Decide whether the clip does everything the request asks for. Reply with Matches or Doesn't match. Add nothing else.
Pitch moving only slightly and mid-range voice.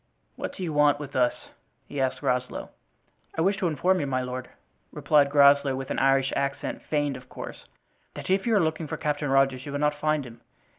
Matches